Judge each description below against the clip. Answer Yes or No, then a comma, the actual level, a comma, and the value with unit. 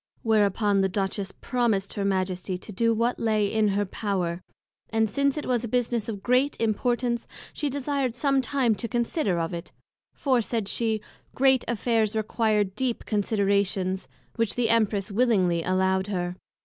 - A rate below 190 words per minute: Yes, average, 160 wpm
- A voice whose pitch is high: Yes, high, 220 Hz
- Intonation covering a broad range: No, average, 3.6 semitones